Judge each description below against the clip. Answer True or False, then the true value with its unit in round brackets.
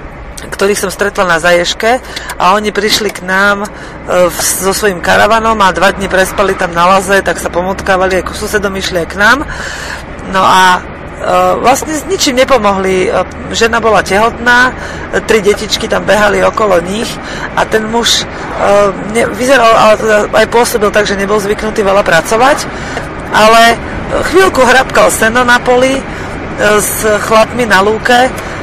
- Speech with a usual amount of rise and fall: True (3.2 semitones)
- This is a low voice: False (210 Hz)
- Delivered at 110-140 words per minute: False (150 wpm)